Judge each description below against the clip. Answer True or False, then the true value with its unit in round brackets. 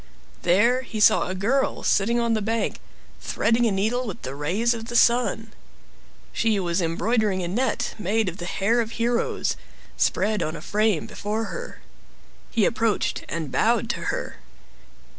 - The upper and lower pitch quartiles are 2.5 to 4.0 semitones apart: True (3.5 semitones)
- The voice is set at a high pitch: True (220 Hz)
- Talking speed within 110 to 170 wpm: True (160 wpm)